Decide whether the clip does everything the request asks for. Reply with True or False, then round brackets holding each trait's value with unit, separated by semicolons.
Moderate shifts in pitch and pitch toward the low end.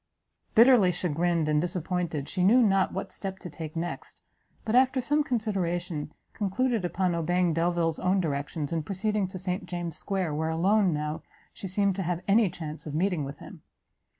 False (3.3 semitones; 180 Hz)